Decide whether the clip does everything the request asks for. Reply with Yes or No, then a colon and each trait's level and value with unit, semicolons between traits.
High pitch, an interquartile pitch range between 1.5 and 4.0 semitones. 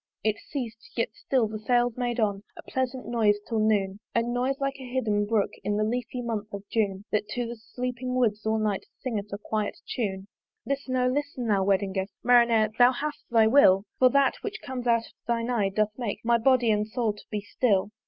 Yes: high, 230 Hz; average, 3.1 semitones